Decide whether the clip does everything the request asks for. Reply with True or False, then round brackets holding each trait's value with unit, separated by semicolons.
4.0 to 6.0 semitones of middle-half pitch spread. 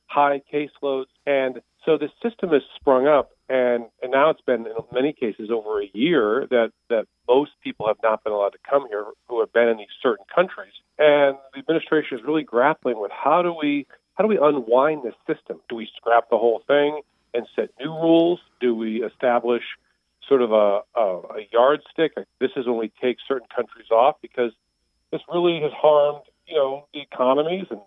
True (5.0 semitones)